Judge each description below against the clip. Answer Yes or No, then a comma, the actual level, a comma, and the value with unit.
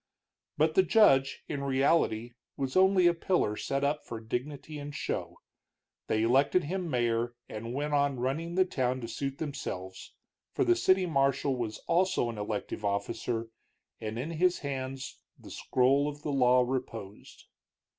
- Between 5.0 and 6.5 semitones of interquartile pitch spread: No, average, 4.5 semitones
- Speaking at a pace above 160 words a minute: No, average, 155 wpm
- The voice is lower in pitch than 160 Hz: Yes, low, 135 Hz